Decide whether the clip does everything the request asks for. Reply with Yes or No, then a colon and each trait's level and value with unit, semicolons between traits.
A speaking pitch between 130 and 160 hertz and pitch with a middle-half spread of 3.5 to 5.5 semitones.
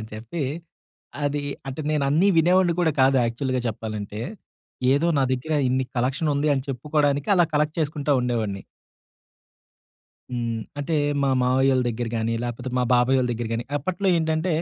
Yes: low, 135 Hz; average, 4.0 semitones